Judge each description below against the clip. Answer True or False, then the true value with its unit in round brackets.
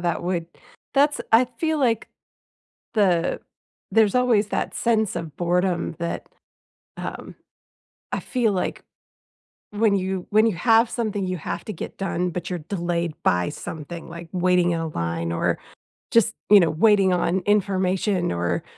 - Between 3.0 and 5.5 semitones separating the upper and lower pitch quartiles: True (3.9 semitones)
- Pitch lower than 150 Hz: False (185 Hz)